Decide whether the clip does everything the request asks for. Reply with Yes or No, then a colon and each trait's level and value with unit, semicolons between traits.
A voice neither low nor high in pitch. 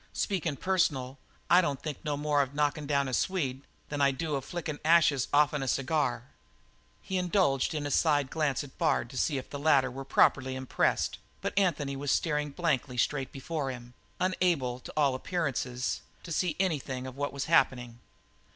Yes: medium, 145 Hz